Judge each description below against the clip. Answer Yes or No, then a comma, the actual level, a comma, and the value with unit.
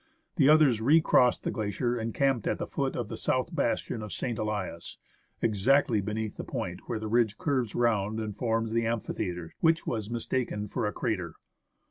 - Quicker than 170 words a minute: Yes, average, 185 wpm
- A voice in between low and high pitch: No, low, 110 Hz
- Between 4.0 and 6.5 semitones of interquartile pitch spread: No, average, 2.7 semitones